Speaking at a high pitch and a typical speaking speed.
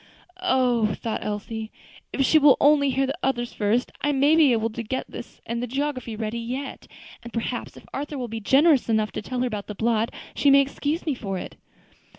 No: high, 245 Hz; fast, 210 wpm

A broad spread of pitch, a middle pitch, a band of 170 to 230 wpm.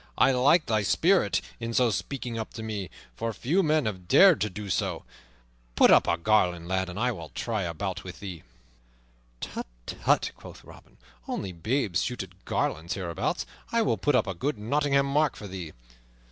No: wide, 6.4 semitones; low, 110 Hz; average, 190 wpm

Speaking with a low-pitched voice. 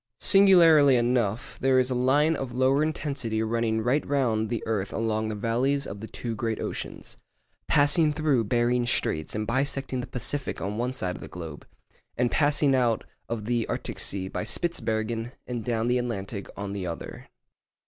Yes: low, 120 Hz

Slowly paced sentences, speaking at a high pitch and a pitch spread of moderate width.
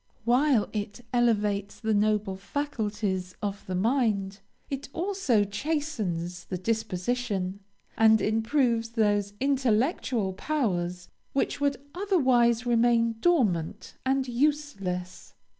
Yes: slow, 100 wpm; high, 225 Hz; average, 4.8 semitones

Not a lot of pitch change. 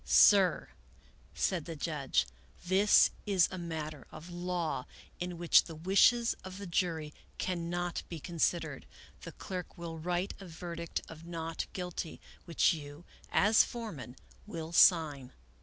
Yes: narrow, 2.2 semitones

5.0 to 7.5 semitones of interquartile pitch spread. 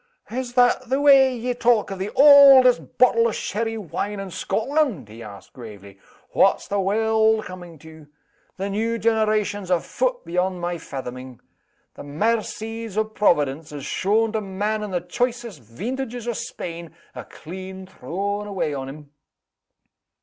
Yes: average, 5.3 semitones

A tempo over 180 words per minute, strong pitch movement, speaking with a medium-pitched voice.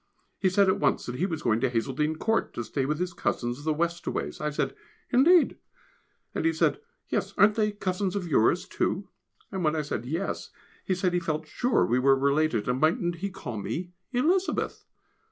Yes: average, 195 wpm; wide, 5.8 semitones; medium, 165 Hz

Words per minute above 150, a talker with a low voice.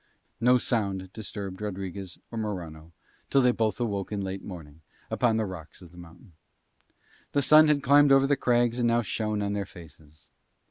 Yes: average, 175 wpm; low, 105 Hz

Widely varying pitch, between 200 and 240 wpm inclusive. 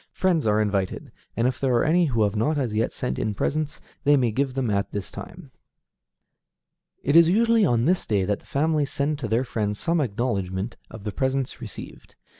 Yes: wide, 6.0 semitones; fast, 205 wpm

